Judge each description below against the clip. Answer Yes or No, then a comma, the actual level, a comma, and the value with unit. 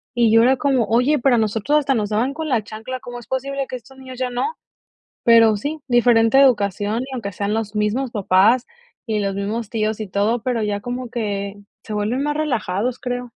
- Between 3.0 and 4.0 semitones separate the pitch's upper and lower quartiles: Yes, average, 3.4 semitones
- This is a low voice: No, high, 235 Hz